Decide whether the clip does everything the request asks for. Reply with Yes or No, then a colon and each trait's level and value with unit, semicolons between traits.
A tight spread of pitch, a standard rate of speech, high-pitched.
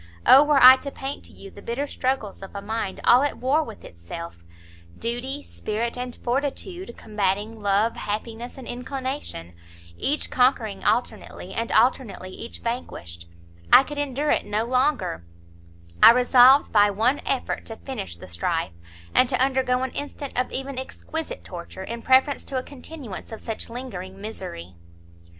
No: average, 4.5 semitones; average, 160 wpm; high, 245 Hz